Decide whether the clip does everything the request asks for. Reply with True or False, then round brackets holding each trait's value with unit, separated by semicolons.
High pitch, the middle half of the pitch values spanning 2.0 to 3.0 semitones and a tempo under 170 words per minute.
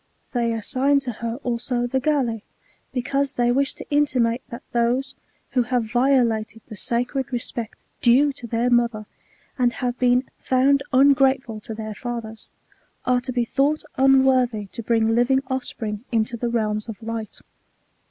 True (245 Hz; 2.4 semitones; 150 wpm)